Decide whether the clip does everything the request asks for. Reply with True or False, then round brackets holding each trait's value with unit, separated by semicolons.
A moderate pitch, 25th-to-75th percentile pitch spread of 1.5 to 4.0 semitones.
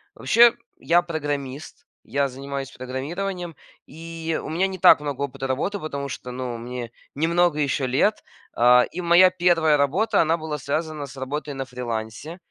False (150 Hz; 4.4 semitones)